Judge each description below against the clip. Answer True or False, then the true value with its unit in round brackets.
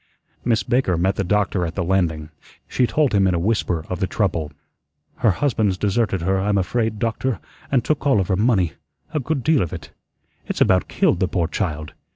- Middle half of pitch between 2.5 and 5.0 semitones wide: True (4.6 semitones)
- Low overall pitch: True (100 Hz)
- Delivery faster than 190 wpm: True (200 wpm)